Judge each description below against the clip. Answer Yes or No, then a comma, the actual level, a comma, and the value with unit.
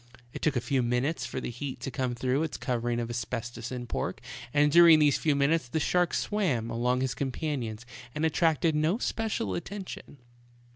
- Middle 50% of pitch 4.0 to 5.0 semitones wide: Yes, average, 4.7 semitones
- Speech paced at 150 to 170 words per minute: No, average, 185 wpm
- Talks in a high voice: No, low, 135 Hz